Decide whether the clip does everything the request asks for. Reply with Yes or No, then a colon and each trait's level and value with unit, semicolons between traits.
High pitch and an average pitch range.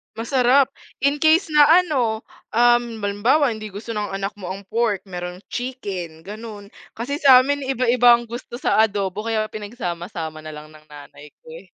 Yes: high, 220 Hz; average, 4.8 semitones